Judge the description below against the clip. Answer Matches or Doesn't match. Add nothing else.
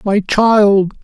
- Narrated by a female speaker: Doesn't match